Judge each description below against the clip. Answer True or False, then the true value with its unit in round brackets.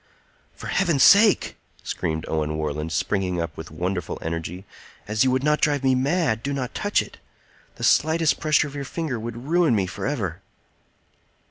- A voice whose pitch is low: True (120 Hz)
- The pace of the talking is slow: False (165 wpm)